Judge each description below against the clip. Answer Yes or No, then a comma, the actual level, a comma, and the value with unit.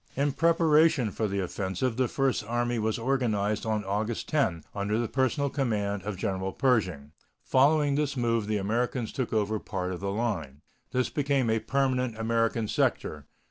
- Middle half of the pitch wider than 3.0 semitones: Yes, average, 4.5 semitones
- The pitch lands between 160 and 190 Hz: No, low, 115 Hz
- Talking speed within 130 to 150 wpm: No, average, 165 wpm